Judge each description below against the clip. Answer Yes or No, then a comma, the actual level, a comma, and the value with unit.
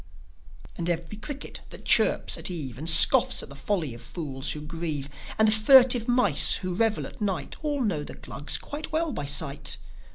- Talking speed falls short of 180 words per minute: No, average, 190 wpm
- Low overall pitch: No, medium, 175 Hz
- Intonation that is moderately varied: No, wide, 7.5 semitones